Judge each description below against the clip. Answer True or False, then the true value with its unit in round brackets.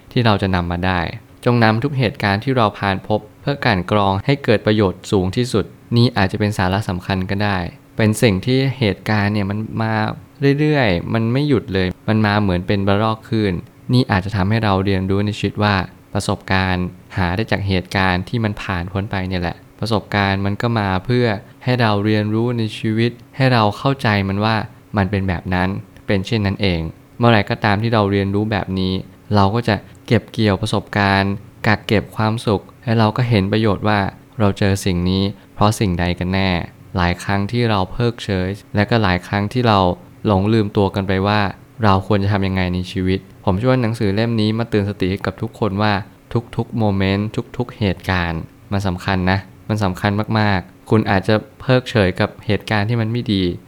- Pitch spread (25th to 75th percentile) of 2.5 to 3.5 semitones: True (2.9 semitones)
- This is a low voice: True (105 Hz)